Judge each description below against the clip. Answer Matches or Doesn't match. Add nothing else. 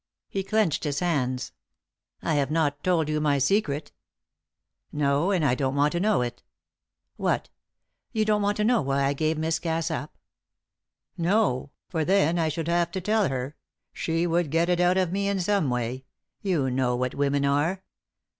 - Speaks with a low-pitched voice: Doesn't match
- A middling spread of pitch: Matches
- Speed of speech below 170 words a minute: Doesn't match